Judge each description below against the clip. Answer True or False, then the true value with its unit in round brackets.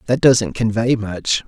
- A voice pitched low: True (110 Hz)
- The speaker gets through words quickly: False (165 wpm)